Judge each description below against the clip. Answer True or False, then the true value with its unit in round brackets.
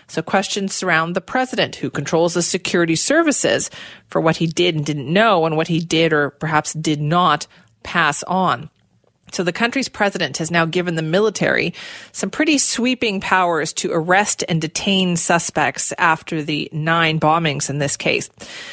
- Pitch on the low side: False (170 Hz)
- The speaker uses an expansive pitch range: False (3.4 semitones)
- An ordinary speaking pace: True (165 wpm)